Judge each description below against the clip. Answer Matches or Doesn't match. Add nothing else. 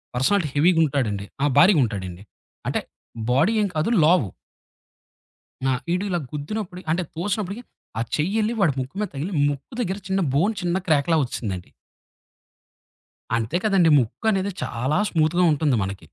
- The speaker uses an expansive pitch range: Matches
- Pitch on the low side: Doesn't match